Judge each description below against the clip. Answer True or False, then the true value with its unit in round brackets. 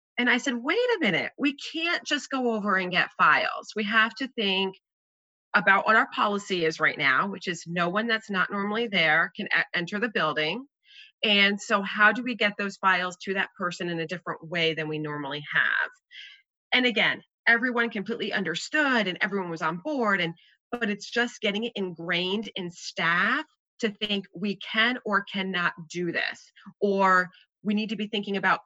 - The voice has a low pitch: False (205 Hz)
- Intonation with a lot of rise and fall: False (4.7 semitones)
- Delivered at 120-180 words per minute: False (190 wpm)